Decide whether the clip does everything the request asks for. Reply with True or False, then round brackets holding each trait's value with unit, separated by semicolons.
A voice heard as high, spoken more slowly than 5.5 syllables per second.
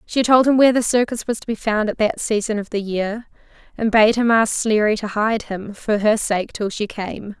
True (220 Hz; 5.0 syllables/s)